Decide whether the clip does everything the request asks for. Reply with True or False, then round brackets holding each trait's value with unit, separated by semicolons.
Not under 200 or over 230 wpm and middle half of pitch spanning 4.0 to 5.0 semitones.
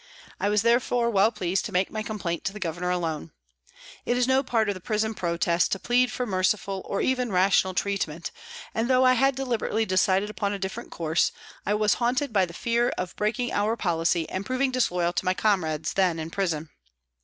True (205 wpm; 4.6 semitones)